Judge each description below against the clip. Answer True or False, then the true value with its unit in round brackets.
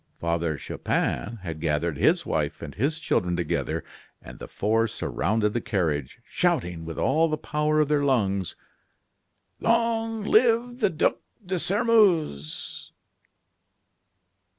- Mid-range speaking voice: False (120 Hz)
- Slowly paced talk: True (125 wpm)